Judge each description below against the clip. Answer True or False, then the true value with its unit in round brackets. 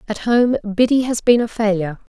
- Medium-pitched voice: False (220 Hz)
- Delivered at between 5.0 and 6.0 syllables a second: True (5.6 syllables/s)